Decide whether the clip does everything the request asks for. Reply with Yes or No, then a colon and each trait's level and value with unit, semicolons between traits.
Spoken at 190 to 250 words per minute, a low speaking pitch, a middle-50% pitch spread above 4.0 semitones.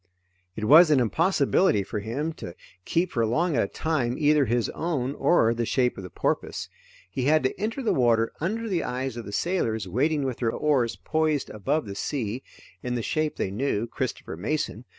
Yes: average, 195 wpm; low, 130 Hz; wide, 5.5 semitones